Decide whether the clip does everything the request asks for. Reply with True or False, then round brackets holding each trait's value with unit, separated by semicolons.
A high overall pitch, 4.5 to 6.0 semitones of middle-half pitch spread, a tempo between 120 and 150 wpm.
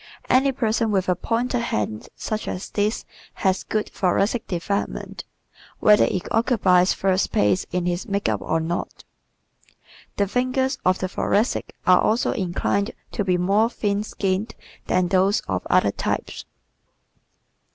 False (200 Hz; 3.5 semitones; 140 wpm)